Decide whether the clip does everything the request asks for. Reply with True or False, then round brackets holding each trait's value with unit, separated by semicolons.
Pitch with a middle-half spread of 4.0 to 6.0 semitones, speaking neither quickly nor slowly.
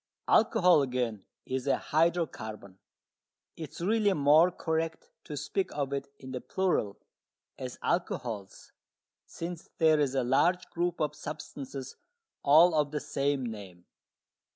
False (4.9 semitones; 130 wpm)